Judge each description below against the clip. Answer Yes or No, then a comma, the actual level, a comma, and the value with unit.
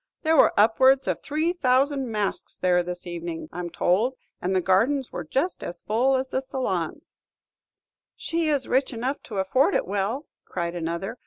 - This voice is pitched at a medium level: No, high, 230 Hz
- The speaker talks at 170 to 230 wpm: Yes, average, 175 wpm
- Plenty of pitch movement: Yes, wide, 7.0 semitones